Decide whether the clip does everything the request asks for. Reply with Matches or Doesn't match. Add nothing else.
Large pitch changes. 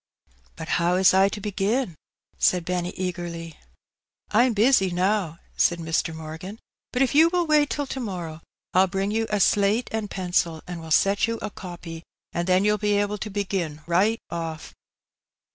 Doesn't match